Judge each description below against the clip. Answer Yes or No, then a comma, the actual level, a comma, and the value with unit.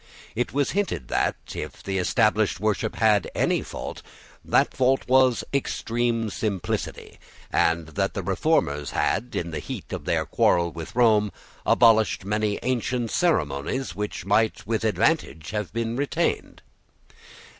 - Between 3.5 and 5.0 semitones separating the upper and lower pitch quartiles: Yes, average, 4.2 semitones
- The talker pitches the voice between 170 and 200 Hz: No, low, 110 Hz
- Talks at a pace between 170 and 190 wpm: No, slow, 135 wpm